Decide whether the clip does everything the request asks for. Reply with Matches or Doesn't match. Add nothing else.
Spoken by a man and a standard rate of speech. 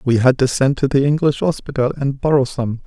Doesn't match